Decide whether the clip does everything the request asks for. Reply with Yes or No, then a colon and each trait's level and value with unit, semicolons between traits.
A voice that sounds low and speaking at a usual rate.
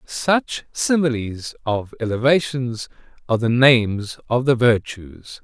No: low, 125 Hz; slow, 110 wpm